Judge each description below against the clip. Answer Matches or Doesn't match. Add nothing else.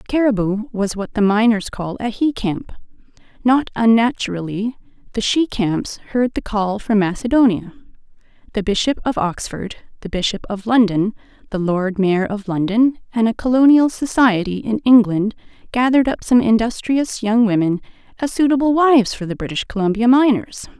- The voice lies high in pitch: Matches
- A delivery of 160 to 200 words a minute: Doesn't match